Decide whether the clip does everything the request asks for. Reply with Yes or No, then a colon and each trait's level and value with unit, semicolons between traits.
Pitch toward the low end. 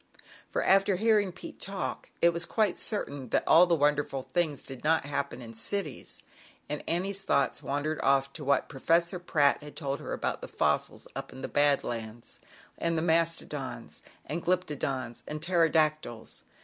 No: medium, 155 Hz